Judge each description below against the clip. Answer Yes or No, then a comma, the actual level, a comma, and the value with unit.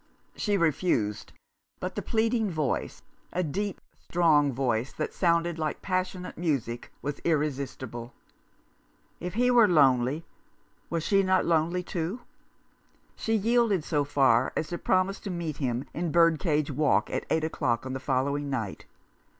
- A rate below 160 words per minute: Yes, average, 150 wpm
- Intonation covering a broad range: No, average, 5.0 semitones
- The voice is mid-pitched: Yes, medium, 160 Hz